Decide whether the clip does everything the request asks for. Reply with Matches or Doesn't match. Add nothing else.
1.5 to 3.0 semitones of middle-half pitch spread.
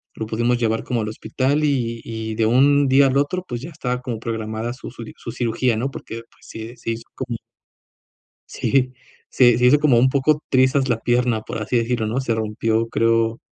Matches